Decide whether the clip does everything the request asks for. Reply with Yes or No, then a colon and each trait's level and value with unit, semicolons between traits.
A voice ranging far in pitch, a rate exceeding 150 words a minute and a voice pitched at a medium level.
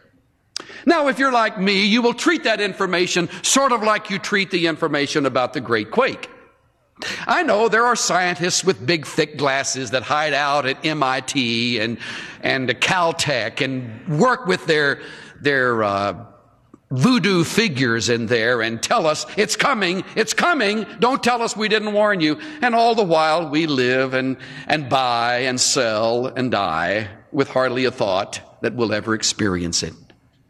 Yes: wide, 8.8 semitones; average, 165 wpm; medium, 155 Hz